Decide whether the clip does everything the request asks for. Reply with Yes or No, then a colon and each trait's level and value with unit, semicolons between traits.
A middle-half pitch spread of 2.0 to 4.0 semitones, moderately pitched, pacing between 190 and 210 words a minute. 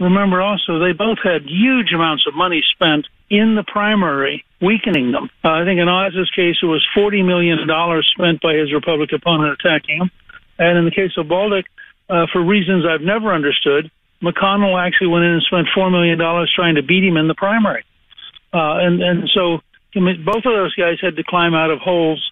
Yes: average, 2.9 semitones; medium, 180 Hz; average, 200 wpm